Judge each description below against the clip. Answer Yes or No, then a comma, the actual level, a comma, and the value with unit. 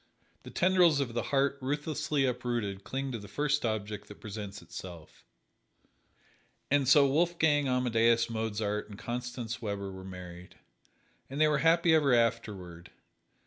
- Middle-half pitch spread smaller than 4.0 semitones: No, wide, 5.6 semitones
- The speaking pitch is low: Yes, low, 120 Hz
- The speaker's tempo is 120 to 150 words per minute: Yes, average, 140 wpm